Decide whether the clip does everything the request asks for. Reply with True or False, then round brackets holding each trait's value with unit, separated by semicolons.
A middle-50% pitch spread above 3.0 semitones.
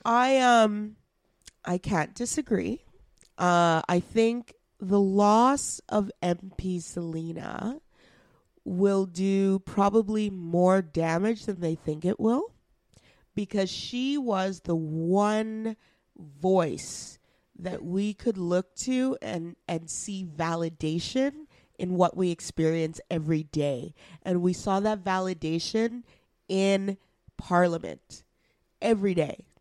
True (4.0 semitones)